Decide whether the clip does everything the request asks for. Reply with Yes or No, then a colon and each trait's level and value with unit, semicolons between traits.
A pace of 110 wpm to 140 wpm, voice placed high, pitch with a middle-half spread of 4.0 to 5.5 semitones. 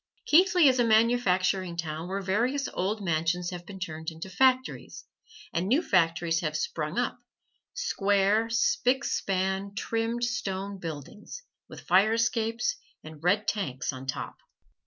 Yes: slow, 135 wpm; high, 195 Hz; average, 5.2 semitones